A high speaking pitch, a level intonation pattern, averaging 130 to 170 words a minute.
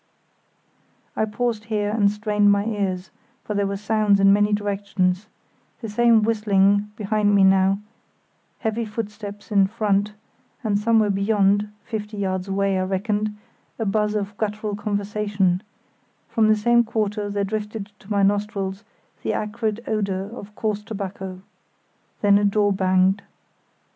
Yes: high, 205 Hz; narrow, 1.3 semitones; slow, 135 wpm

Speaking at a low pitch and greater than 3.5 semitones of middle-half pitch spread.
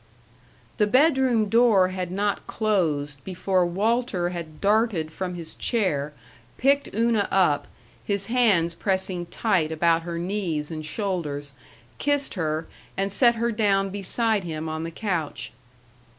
No: high, 190 Hz; average, 4.9 semitones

